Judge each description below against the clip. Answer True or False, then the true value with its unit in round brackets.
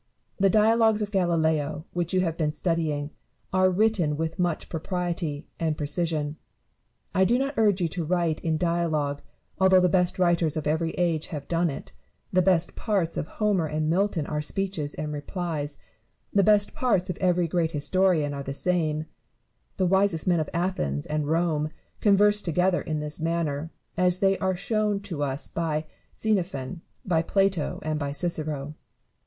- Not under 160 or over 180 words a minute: True (170 wpm)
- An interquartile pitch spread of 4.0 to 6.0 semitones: False (3.5 semitones)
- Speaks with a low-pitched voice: False (170 Hz)